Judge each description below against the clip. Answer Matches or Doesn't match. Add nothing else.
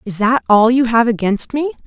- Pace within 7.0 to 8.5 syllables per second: Doesn't match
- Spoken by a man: Doesn't match